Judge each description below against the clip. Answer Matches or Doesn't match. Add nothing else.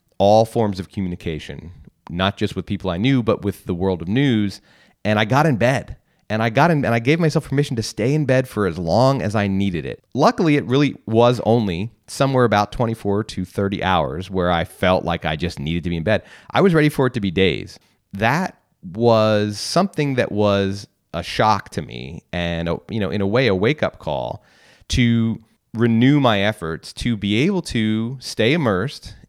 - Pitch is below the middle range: Matches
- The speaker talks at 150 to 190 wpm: Doesn't match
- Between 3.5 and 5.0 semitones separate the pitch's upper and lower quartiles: Matches